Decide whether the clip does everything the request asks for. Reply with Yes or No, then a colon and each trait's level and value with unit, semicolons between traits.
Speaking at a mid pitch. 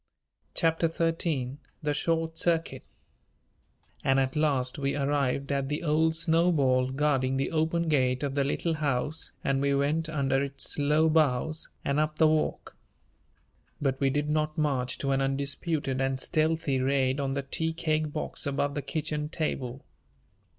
Yes: medium, 145 Hz